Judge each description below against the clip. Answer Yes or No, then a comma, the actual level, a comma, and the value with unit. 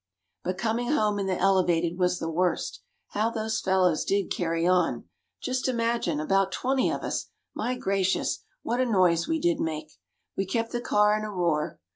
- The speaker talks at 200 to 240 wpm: No, average, 180 wpm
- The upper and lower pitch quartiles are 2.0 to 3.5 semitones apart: No, average, 4.4 semitones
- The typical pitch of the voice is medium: No, high, 195 Hz